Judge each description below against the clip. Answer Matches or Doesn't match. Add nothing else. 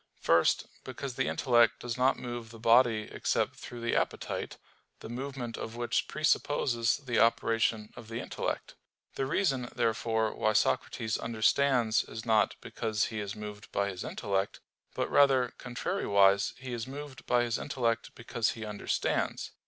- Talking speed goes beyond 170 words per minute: Doesn't match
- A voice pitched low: Matches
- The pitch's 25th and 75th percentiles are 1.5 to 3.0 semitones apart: Matches